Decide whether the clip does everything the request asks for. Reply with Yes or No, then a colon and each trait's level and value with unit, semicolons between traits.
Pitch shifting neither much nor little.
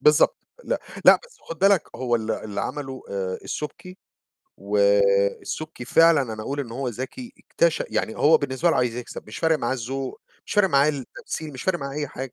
No: wide, 5.8 semitones